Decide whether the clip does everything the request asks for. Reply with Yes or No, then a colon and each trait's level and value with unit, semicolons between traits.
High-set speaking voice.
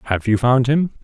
No: low, 125 Hz